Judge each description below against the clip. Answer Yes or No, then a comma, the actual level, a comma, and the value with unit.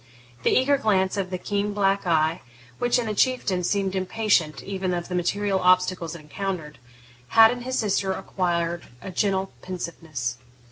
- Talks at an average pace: Yes, average, 160 wpm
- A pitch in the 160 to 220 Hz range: Yes, high, 190 Hz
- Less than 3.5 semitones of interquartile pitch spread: Yes, average, 2.9 semitones